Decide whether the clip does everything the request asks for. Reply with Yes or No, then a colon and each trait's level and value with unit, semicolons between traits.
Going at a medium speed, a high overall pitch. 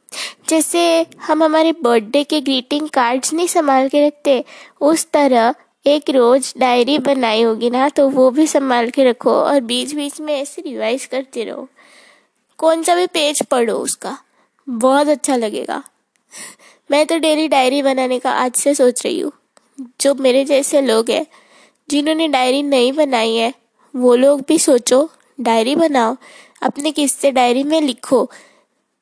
Yes: average, 155 wpm; very high, 275 Hz